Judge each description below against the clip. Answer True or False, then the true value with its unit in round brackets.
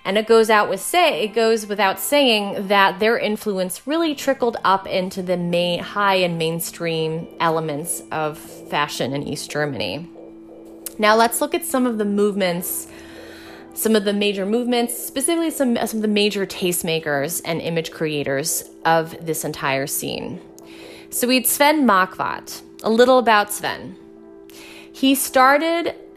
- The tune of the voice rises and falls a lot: True (6.0 semitones)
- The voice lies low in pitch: False (190 Hz)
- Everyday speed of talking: True (150 wpm)